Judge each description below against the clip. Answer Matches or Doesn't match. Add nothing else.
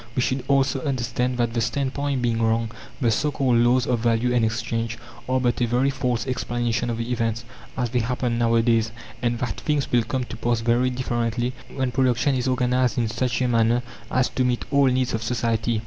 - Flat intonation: Matches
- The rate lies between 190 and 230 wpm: Matches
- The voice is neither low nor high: Doesn't match